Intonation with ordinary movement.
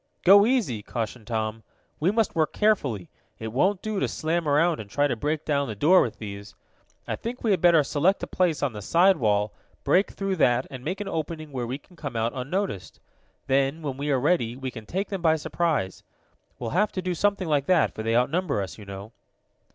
No: wide, 7.6 semitones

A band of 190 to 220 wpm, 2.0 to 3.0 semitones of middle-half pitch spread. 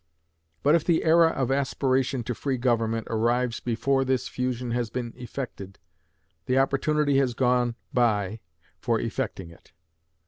No: average, 140 wpm; narrow, 2.5 semitones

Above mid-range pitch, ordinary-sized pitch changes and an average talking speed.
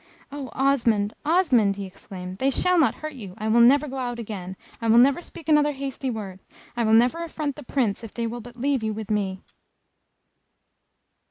Yes: high, 240 Hz; average, 4.6 semitones; average, 195 wpm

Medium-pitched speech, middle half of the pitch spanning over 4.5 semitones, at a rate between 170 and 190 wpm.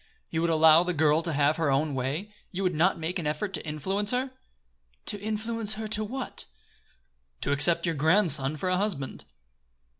Yes: medium, 170 Hz; average, 5.2 semitones; average, 185 wpm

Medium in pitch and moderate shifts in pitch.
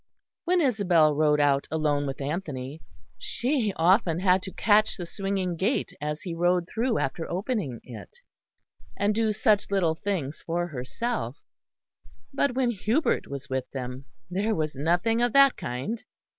No: medium, 175 Hz; wide, 6.4 semitones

